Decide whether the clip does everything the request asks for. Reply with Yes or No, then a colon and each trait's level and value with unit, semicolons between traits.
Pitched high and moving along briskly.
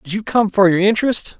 Yes: high, 205 Hz; fast, 260 wpm